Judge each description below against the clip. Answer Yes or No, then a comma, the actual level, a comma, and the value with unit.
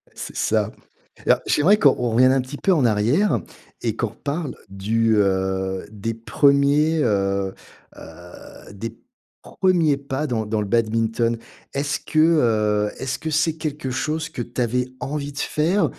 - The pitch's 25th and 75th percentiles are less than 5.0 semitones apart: No, wide, 5.6 semitones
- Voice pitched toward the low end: Yes, low, 125 Hz